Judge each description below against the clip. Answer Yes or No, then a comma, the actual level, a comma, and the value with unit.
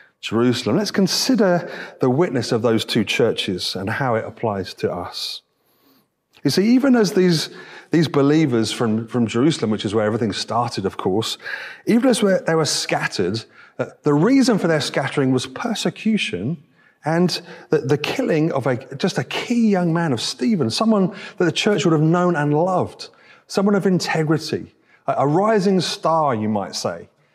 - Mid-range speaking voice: Yes, medium, 165 Hz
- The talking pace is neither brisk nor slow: Yes, average, 170 wpm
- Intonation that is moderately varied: No, wide, 6.0 semitones